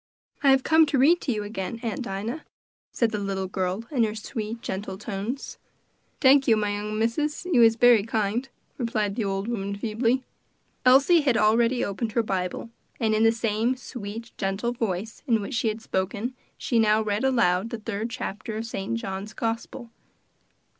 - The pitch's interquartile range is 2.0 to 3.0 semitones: Yes, average, 2.7 semitones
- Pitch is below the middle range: No, high, 225 Hz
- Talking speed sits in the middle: Yes, average, 180 wpm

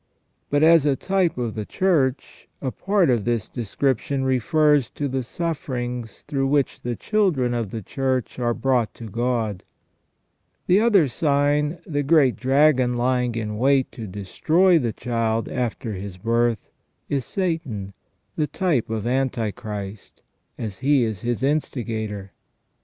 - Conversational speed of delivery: Yes, average, 145 wpm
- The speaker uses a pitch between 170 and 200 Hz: No, low, 125 Hz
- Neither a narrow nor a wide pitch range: Yes, average, 4.2 semitones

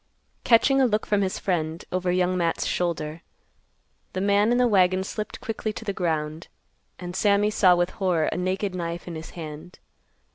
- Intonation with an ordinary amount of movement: Yes, average, 3.2 semitones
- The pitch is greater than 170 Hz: Yes, medium, 185 Hz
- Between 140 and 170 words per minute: No, average, 180 wpm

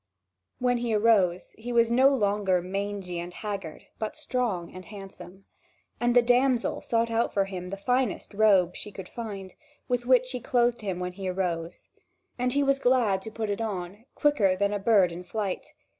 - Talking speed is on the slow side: No, average, 185 wpm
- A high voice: Yes, high, 205 Hz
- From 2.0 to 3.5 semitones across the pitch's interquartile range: No, average, 4.3 semitones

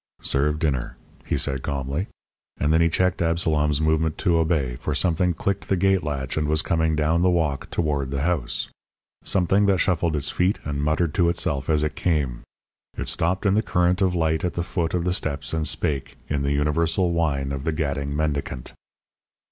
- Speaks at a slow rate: No, average, 195 wpm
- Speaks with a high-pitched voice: No, very low, 80 Hz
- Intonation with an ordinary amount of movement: Yes, average, 3.2 semitones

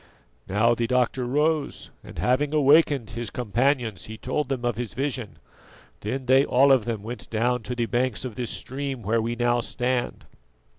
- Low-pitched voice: Yes, low, 125 Hz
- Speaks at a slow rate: No, average, 180 wpm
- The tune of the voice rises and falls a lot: No, narrow, 2.5 semitones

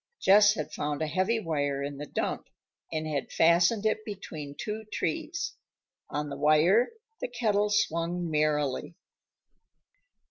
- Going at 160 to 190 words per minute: No, slow, 135 wpm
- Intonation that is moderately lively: No, wide, 6.0 semitones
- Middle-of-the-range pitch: Yes, medium, 170 Hz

